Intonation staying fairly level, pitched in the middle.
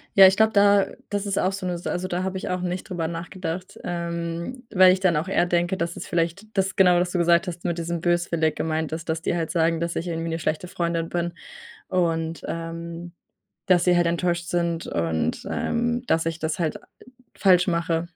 Yes: narrow, 1.7 semitones; medium, 170 Hz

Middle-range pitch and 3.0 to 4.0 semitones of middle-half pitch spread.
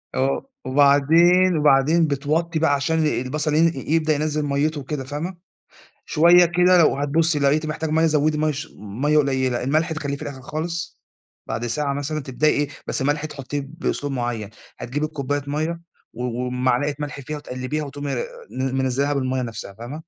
No: medium, 145 Hz; narrow, 2.6 semitones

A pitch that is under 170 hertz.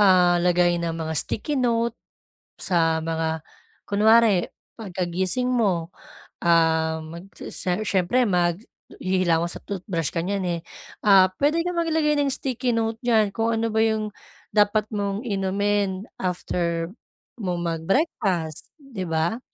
No: high, 190 Hz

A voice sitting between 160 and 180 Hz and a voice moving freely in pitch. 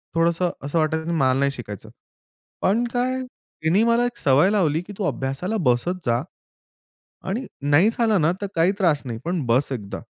Yes: medium, 165 Hz; wide, 6.7 semitones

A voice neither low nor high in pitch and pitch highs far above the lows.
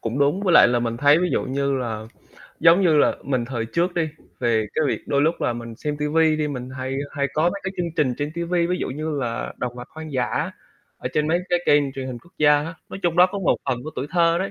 No: medium, 150 Hz; average, 4.7 semitones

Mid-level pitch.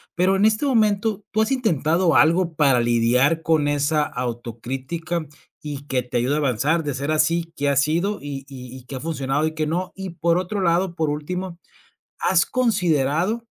Yes: medium, 160 Hz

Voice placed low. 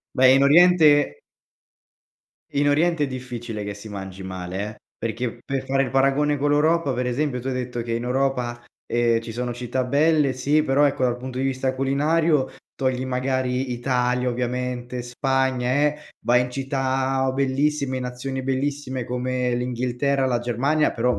Yes: low, 130 Hz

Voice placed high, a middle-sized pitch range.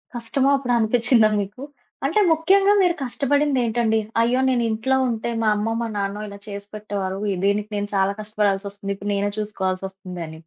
Yes: high, 215 Hz; average, 3.5 semitones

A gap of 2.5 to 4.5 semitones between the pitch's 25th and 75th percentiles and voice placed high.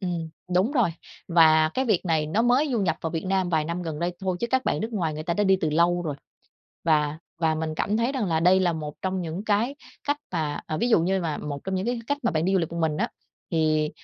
No: average, 4.2 semitones; medium, 175 Hz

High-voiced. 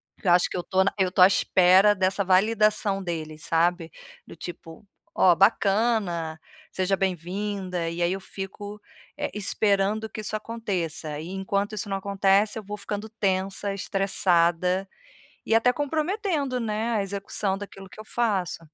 Yes: high, 195 Hz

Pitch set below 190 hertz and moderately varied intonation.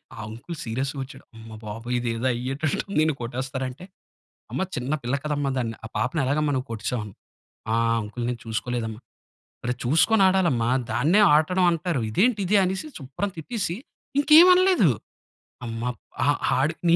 No: low, 135 Hz; wide, 6.5 semitones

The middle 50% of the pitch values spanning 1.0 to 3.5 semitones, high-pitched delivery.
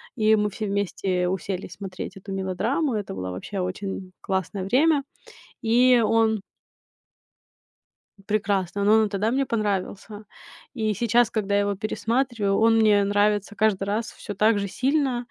Yes: narrow, 2.5 semitones; high, 210 Hz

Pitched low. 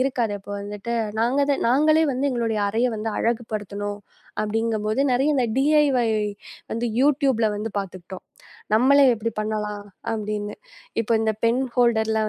No: high, 225 Hz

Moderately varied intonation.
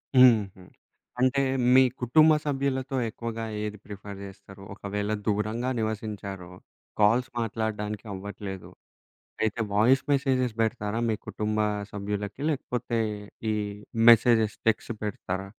Yes: average, 3.2 semitones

